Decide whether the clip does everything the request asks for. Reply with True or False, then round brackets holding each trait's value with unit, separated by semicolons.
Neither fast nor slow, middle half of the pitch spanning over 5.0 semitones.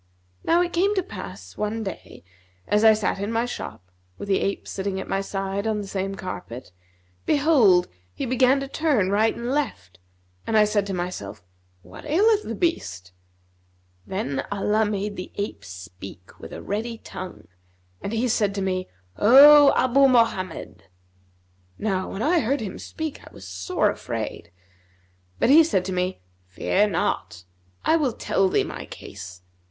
True (165 wpm; 5.5 semitones)